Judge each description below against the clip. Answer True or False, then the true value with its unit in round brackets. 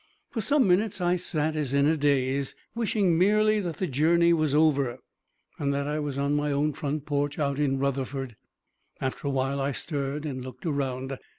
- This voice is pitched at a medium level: True (145 Hz)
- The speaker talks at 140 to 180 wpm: False (190 wpm)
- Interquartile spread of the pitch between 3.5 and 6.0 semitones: False (3.1 semitones)